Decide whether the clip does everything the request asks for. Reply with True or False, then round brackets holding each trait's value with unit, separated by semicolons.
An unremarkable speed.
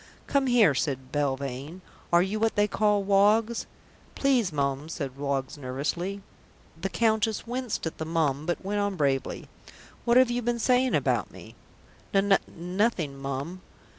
True (150 wpm)